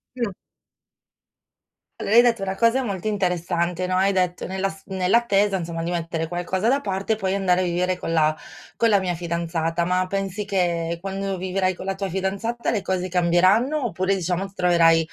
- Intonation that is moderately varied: No, narrow, 2.1 semitones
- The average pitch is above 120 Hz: Yes, medium, 185 Hz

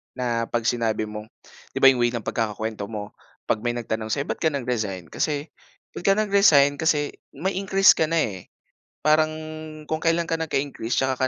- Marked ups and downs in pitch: Yes, wide, 5.9 semitones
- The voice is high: No, low, 130 Hz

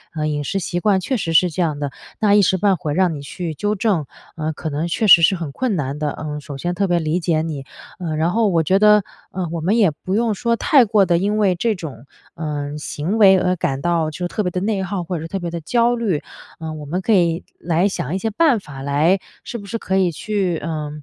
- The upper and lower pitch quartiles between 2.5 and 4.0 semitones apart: No, average, 4.4 semitones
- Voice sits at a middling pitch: Yes, medium, 175 Hz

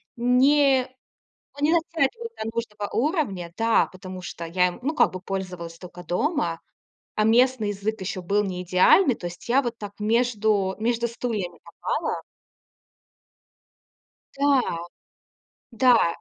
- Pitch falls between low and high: No, high, 220 Hz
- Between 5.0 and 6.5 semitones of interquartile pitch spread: Yes, wide, 5.6 semitones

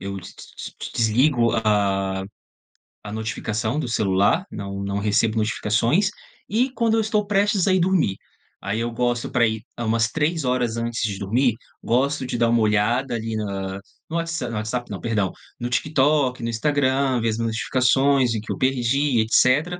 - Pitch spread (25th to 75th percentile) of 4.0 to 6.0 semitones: Yes, average, 4.3 semitones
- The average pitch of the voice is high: No, low, 120 Hz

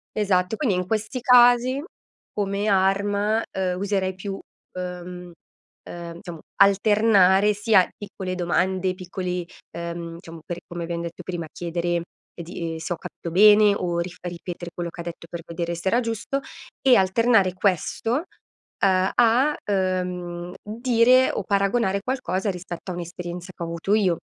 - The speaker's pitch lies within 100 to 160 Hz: No, medium, 185 Hz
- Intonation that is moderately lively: Yes, average, 3.1 semitones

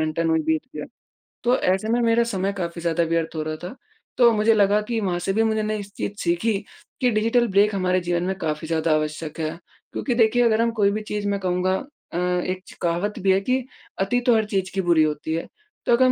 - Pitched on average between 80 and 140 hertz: No, high, 190 Hz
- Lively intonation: No, average, 4.4 semitones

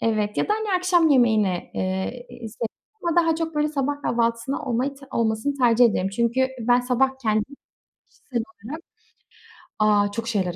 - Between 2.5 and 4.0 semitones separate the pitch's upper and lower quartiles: No, average, 4.7 semitones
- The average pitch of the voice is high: Yes, high, 240 Hz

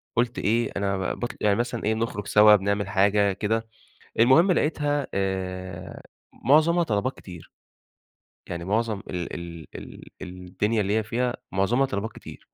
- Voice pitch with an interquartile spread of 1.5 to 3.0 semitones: No, average, 3.7 semitones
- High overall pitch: No, low, 105 Hz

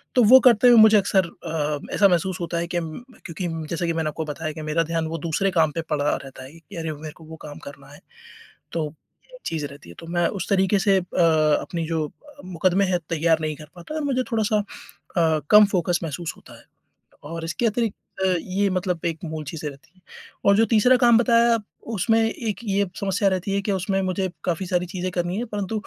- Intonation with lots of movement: No, average, 3.8 semitones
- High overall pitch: No, medium, 175 Hz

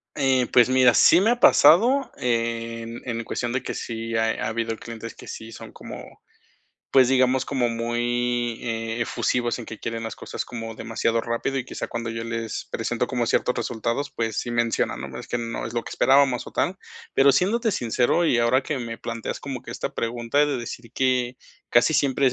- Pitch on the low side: Yes, low, 120 Hz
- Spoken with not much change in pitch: Yes, narrow, 2.1 semitones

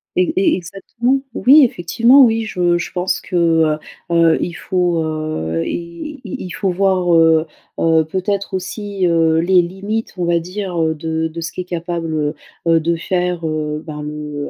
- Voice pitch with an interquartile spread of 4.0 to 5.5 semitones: No, average, 3.1 semitones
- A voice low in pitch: No, medium, 175 Hz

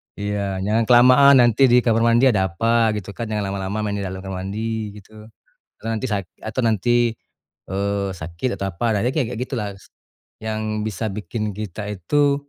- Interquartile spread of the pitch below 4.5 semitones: Yes, average, 2.9 semitones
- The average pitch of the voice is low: Yes, low, 110 Hz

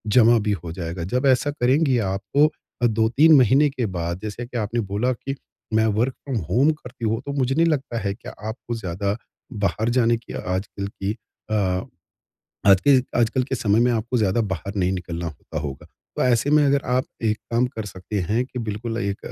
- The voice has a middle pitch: No, low, 115 Hz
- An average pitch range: Yes, average, 4.5 semitones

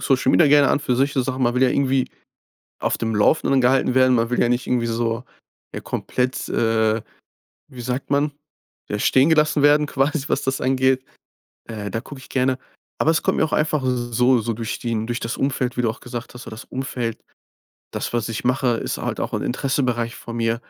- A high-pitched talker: No, low, 125 Hz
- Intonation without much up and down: Yes, narrow, 2.3 semitones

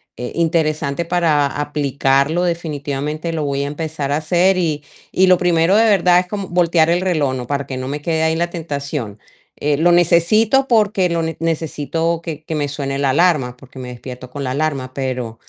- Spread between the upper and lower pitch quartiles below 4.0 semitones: Yes, average, 3.5 semitones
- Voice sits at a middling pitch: Yes, medium, 155 Hz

